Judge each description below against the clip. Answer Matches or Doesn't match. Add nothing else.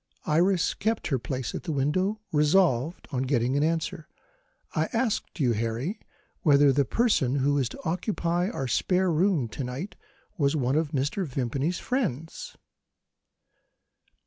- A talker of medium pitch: Matches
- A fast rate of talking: Doesn't match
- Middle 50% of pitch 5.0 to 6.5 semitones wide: Matches